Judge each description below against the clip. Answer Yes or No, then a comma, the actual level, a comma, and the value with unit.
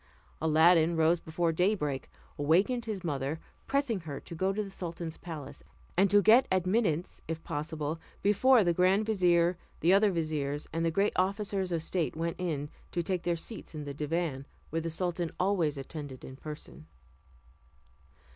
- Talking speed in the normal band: Yes, average, 165 wpm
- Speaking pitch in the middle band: Yes, medium, 170 Hz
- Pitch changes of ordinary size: Yes, average, 3.5 semitones